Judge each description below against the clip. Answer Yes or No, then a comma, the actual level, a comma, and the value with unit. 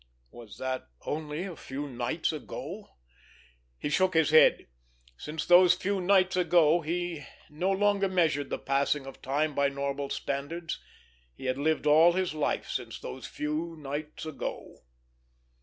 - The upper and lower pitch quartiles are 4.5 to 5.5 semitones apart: No, average, 3.8 semitones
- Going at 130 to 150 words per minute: Yes, average, 145 wpm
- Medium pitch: Yes, medium, 155 Hz